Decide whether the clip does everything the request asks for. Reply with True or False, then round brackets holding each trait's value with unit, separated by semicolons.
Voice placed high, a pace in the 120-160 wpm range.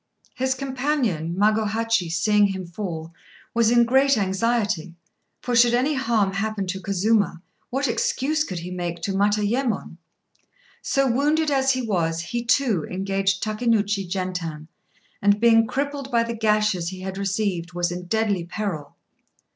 True (210 Hz; 145 wpm)